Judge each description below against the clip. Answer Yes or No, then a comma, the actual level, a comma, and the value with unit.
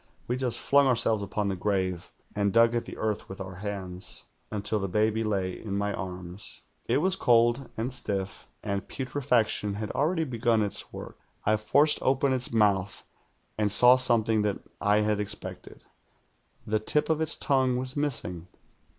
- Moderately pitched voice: No, low, 110 Hz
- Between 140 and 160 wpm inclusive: No, average, 170 wpm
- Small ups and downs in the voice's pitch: No, average, 3.9 semitones